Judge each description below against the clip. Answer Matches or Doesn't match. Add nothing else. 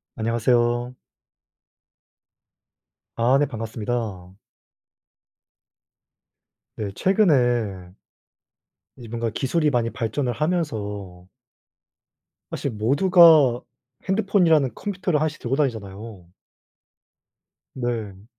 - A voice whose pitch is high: Doesn't match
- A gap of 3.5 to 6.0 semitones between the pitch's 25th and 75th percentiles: Matches